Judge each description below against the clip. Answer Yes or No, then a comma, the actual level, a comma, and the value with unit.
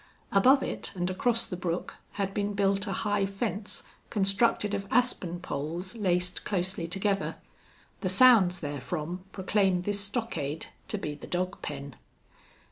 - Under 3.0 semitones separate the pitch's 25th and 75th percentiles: Yes, narrow, 2.6 semitones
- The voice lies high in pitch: Yes, high, 195 Hz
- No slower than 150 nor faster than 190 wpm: No, average, 140 wpm